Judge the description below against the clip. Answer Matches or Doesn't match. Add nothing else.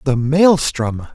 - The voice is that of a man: Matches